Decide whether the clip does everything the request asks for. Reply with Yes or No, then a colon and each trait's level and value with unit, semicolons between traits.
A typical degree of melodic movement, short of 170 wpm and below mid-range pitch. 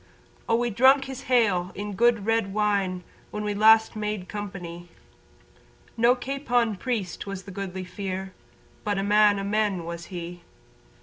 No: average, 3.3 semitones; average, 160 wpm; high, 205 Hz